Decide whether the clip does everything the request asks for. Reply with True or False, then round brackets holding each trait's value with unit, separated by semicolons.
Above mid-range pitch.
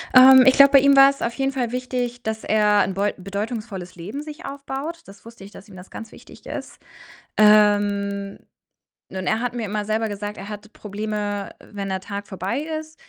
True (215 Hz)